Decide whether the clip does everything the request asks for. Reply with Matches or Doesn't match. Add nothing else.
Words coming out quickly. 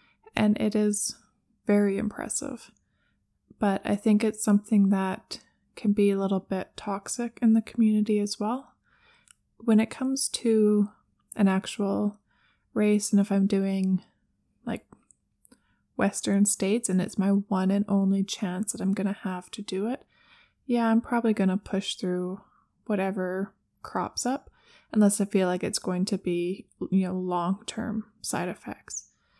Doesn't match